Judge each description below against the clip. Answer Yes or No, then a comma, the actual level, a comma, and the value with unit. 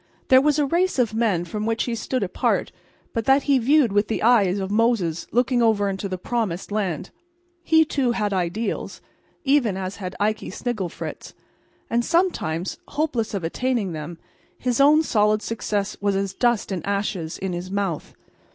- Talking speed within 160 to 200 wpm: Yes, average, 170 wpm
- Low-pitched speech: No, high, 215 Hz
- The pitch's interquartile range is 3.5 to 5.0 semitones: Yes, average, 4.4 semitones